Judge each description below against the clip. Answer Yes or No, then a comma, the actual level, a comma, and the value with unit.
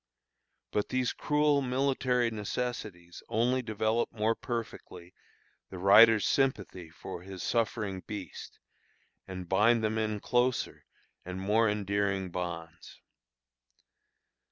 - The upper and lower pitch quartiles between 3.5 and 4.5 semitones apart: Yes, average, 4.1 semitones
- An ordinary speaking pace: No, slow, 105 wpm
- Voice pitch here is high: No, low, 105 Hz